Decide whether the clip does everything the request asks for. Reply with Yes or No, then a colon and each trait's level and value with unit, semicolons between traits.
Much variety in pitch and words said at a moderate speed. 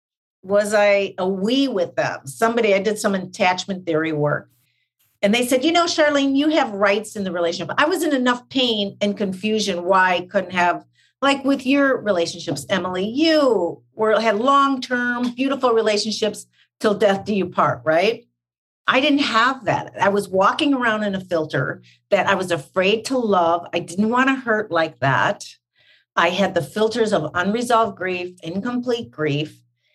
Yes: wide, 5.7 semitones; average, 175 wpm